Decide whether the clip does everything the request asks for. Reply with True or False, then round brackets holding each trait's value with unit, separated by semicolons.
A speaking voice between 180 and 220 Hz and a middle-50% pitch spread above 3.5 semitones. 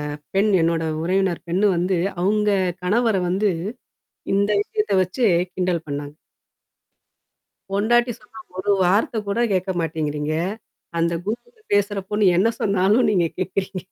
False (195 Hz; 3.2 semitones)